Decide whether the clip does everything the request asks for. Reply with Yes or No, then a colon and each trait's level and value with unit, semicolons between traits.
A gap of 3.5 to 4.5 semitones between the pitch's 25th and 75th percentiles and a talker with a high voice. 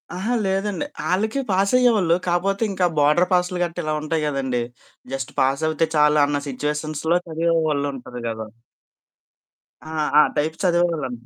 No: average, 3.9 semitones; medium, 160 Hz